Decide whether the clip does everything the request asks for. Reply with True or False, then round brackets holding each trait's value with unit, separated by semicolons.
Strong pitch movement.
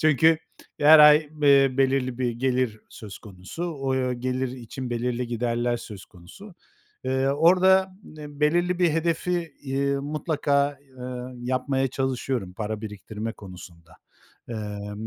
False (4.1 semitones)